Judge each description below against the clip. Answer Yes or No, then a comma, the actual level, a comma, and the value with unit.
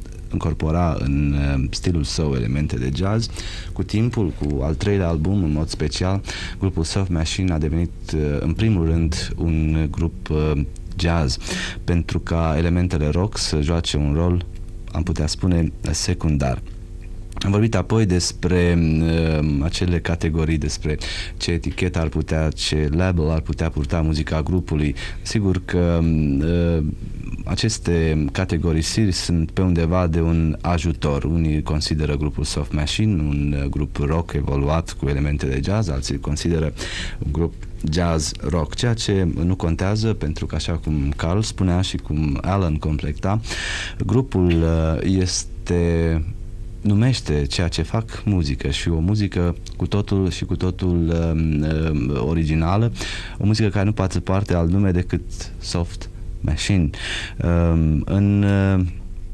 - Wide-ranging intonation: No, average, 3.1 semitones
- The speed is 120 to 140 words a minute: Yes, average, 135 wpm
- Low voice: Yes, very low, 85 Hz